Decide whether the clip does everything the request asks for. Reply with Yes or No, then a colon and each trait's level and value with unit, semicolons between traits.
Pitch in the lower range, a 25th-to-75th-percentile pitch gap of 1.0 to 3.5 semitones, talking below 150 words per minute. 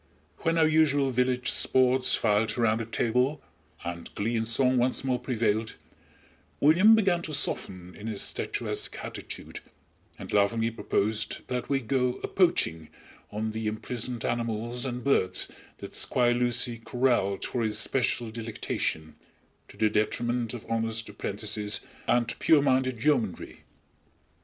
Yes: low, 120 Hz; average, 2.9 semitones; average, 140 wpm